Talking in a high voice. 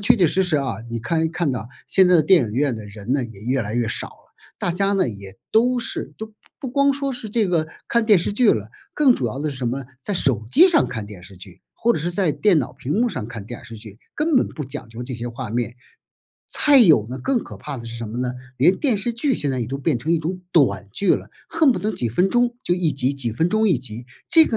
No: medium, 145 Hz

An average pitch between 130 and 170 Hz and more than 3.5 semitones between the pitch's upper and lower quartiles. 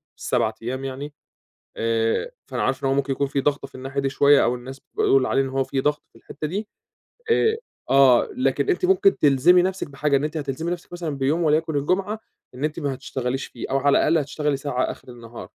No: medium, 140 Hz; average, 3.0 semitones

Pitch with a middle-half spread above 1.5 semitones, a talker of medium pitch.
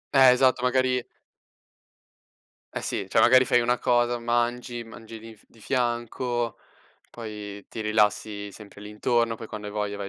No: narrow, 2.4 semitones; low, 115 Hz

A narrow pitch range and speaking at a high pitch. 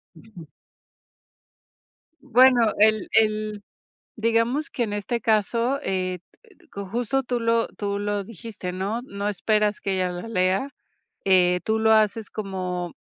No: average, 3.1 semitones; high, 215 Hz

